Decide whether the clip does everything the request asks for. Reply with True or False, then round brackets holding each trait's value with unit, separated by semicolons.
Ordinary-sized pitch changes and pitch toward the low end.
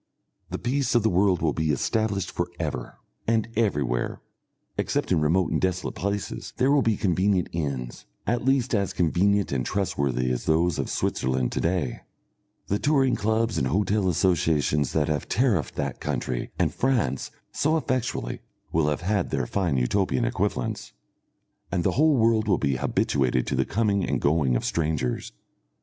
False (7.4 semitones; 90 Hz)